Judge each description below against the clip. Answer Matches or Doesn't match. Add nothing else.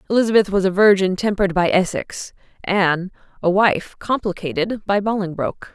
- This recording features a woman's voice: Matches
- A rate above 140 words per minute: Doesn't match